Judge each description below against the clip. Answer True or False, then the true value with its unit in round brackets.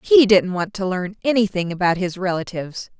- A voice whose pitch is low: False (195 Hz)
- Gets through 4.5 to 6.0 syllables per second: True (5.5 syllables/s)